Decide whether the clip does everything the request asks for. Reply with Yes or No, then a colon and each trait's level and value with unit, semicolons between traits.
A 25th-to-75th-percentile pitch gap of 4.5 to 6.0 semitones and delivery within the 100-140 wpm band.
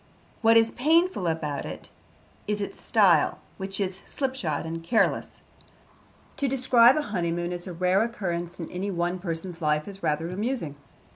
No: average, 5.2 semitones; average, 155 wpm